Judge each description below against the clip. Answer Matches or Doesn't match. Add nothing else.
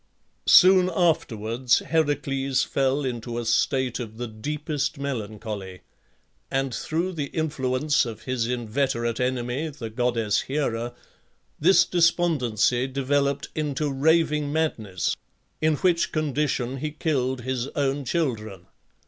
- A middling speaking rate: Doesn't match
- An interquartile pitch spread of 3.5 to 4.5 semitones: Matches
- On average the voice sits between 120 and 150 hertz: Matches